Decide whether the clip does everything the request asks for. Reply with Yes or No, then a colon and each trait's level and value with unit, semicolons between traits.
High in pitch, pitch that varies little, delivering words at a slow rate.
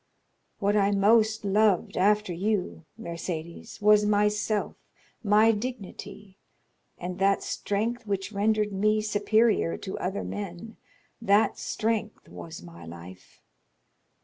Yes: high, 205 Hz; narrow, 2.2 semitones; slow, 110 wpm